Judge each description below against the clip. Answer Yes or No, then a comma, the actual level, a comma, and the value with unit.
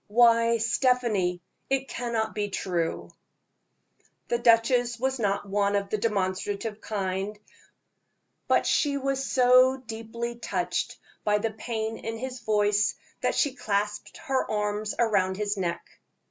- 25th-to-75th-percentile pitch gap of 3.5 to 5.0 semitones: No, average, 2.9 semitones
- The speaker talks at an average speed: No, slow, 130 wpm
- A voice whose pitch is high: Yes, high, 220 Hz